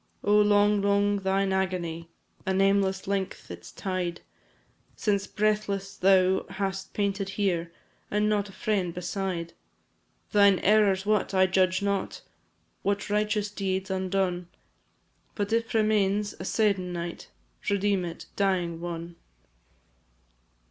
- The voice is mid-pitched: No, high, 195 Hz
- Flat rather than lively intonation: Yes, narrow, 1.7 semitones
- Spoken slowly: Yes, slow, 115 wpm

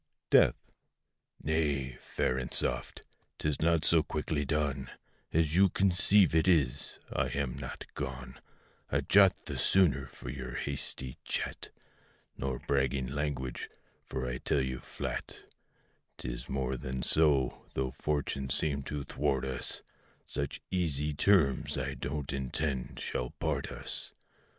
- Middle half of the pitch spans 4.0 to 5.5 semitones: No, average, 2.9 semitones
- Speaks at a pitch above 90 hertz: No, very low, 70 Hz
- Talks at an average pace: No, slow, 130 wpm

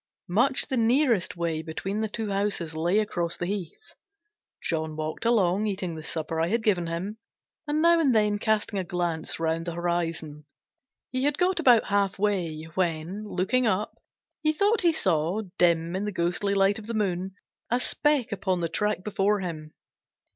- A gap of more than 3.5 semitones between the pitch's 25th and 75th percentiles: Yes, average, 4.4 semitones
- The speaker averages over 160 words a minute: Yes, average, 175 wpm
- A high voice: Yes, high, 195 Hz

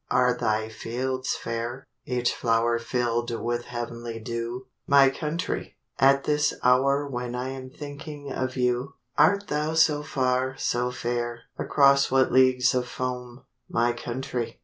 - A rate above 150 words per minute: No, average, 140 wpm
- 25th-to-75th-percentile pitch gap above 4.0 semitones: No, narrow, 2.4 semitones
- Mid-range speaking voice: No, low, 125 Hz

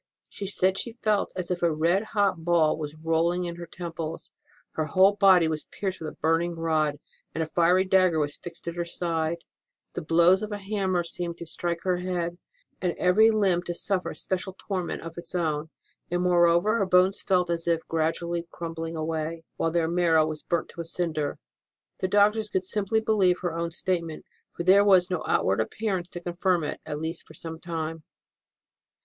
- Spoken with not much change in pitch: Yes, narrow, 2.3 semitones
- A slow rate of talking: No, average, 195 wpm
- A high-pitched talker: No, medium, 175 Hz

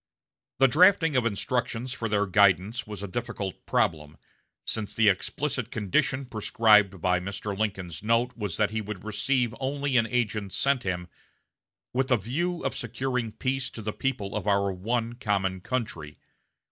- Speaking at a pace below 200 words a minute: Yes, average, 160 wpm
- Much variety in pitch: No, average, 4.2 semitones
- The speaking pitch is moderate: No, low, 110 Hz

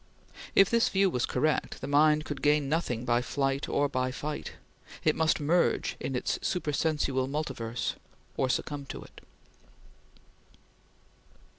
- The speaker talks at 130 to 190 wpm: Yes, slow, 135 wpm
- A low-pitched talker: No, medium, 145 Hz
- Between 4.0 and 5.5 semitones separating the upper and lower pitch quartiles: No, average, 2.9 semitones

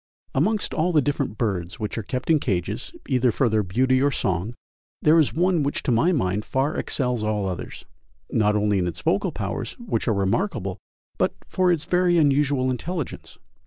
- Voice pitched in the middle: No, low, 130 Hz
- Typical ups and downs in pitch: No, wide, 6.8 semitones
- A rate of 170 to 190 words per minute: Yes, average, 185 wpm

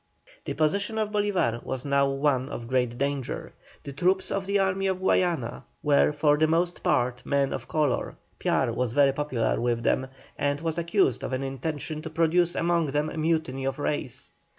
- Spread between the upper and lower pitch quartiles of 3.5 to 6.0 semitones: Yes, average, 4.2 semitones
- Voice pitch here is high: No, medium, 150 Hz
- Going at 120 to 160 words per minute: No, average, 185 wpm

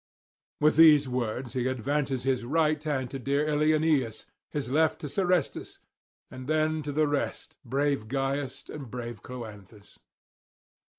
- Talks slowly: Yes, slow, 130 wpm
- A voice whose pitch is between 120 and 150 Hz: Yes, medium, 140 Hz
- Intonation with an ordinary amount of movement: Yes, average, 3.2 semitones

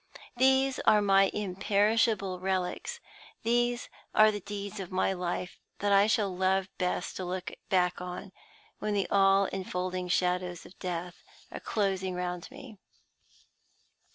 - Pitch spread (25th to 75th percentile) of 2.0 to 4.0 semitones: Yes, narrow, 2.4 semitones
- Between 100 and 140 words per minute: Yes, slow, 135 wpm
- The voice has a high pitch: Yes, high, 195 Hz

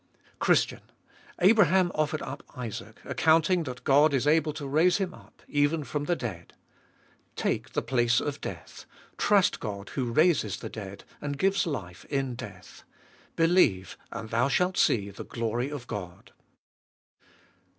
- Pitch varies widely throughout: Yes, wide, 5.9 semitones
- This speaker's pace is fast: No, average, 145 wpm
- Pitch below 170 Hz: Yes, medium, 140 Hz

